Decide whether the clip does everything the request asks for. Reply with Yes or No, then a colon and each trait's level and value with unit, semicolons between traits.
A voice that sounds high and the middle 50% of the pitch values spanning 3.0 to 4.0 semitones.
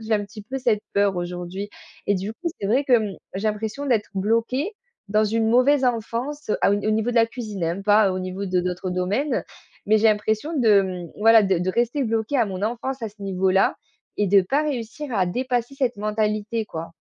Yes: high, 215 Hz; average, 3.5 semitones